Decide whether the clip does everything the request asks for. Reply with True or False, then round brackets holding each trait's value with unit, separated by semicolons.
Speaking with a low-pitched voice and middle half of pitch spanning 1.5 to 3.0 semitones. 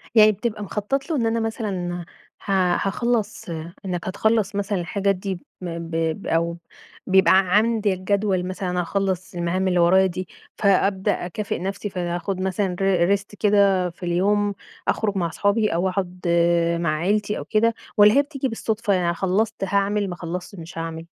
False (195 Hz; 2.7 semitones)